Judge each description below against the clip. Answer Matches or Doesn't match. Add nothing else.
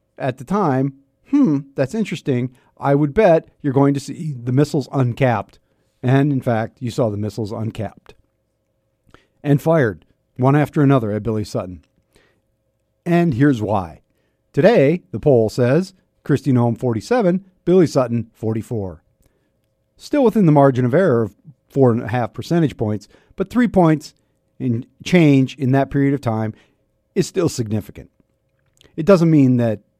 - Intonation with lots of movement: Doesn't match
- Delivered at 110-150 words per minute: Matches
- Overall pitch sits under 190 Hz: Matches